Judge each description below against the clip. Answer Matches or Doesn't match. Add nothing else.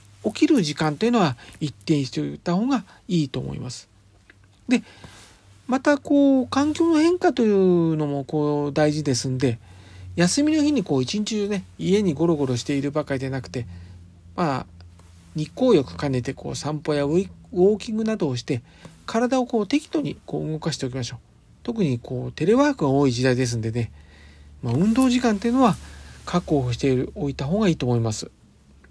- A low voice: Doesn't match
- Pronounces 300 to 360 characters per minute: Matches